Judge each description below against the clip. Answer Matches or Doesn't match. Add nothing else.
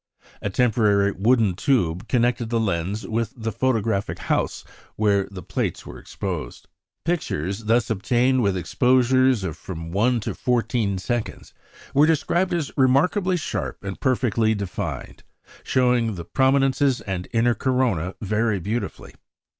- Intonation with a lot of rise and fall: Doesn't match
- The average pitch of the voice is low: Matches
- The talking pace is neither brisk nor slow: Doesn't match